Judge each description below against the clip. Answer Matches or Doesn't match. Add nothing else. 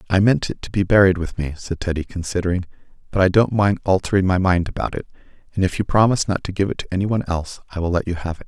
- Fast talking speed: Matches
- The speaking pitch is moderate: Doesn't match